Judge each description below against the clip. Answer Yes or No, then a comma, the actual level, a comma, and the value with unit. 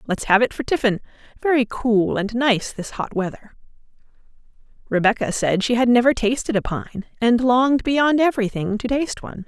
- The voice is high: Yes, high, 230 Hz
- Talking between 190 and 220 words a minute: No, average, 170 wpm